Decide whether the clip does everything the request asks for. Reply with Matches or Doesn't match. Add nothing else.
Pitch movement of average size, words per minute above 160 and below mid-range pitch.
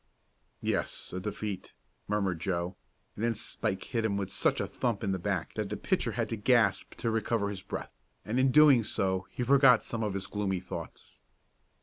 Matches